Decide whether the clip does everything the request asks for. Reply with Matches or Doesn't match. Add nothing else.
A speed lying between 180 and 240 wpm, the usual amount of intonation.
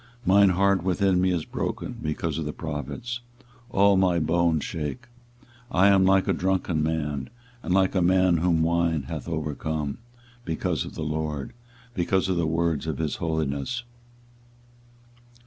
Doesn't match